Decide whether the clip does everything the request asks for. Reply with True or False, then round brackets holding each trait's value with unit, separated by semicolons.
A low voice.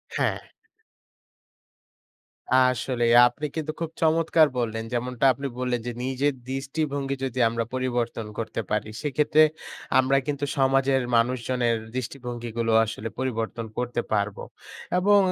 True (130 Hz)